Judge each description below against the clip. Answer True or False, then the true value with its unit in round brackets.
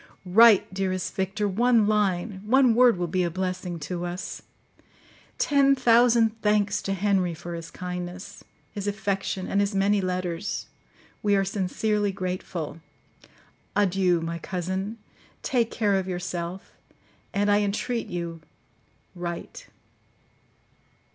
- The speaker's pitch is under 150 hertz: False (195 Hz)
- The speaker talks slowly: True (115 wpm)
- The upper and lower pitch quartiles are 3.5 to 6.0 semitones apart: False (2.8 semitones)